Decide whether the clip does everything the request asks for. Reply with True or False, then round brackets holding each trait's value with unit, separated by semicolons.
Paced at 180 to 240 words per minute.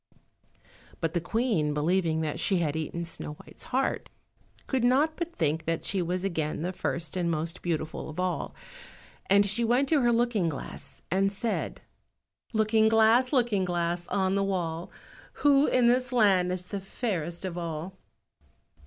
False (160 wpm)